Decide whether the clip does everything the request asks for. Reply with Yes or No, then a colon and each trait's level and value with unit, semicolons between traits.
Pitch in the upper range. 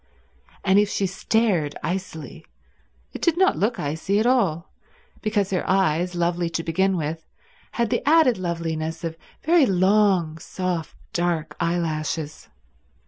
No: medium, 180 Hz